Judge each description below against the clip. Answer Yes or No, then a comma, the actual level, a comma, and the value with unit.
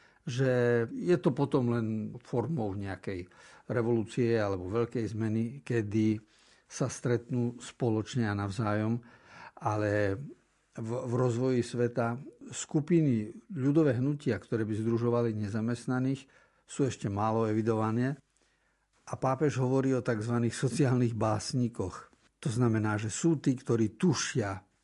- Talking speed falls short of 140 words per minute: Yes, average, 115 wpm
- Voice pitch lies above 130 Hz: No, low, 120 Hz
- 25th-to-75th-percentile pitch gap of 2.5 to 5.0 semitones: Yes, average, 2.9 semitones